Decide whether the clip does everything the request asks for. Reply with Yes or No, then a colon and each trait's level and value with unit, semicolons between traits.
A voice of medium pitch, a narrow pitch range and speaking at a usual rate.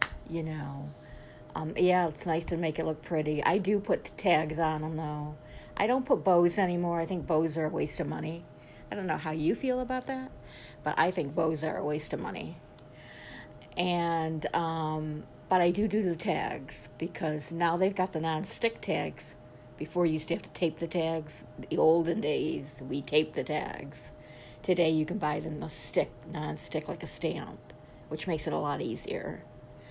Yes: medium, 160 Hz; narrow, 2.2 semitones; average, 195 wpm